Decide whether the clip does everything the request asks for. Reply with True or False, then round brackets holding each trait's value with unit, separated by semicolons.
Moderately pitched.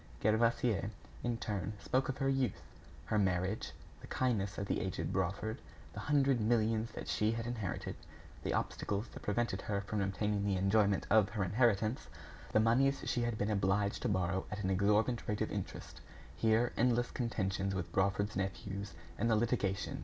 False (105 Hz)